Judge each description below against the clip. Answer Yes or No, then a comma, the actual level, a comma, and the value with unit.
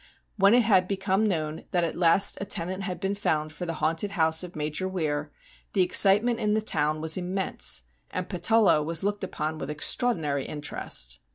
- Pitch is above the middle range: No, medium, 180 Hz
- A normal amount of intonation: Yes, average, 4.3 semitones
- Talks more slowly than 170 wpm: No, average, 190 wpm